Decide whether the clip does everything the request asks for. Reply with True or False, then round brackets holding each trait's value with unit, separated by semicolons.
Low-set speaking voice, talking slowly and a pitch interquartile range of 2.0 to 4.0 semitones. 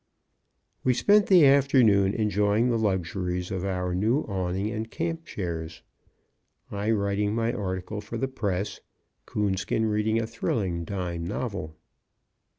True (105 Hz; 130 wpm; 3.6 semitones)